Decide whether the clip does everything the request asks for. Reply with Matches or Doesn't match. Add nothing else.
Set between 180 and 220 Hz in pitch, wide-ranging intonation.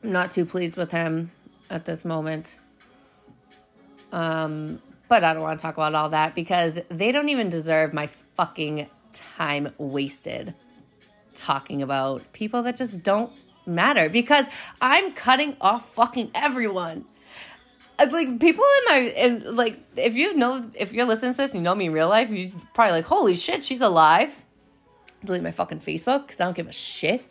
Matches